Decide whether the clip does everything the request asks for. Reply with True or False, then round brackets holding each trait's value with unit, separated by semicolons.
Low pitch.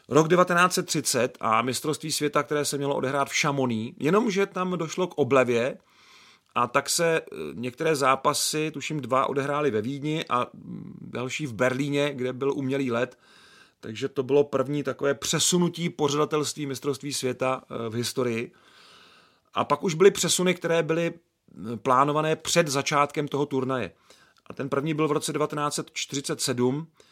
False (145 Hz)